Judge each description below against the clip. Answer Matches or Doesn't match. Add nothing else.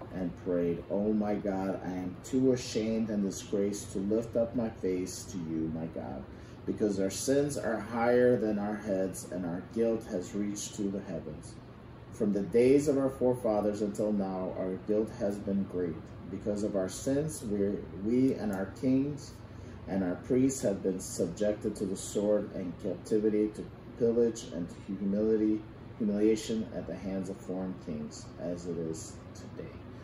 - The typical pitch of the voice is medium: Doesn't match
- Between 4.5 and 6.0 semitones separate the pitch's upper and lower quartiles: Doesn't match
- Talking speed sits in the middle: Matches